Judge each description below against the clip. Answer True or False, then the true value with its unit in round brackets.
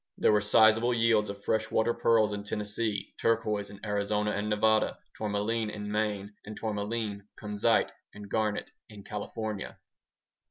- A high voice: False (105 Hz)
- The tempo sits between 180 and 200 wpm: False (135 wpm)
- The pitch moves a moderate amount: False (1.2 semitones)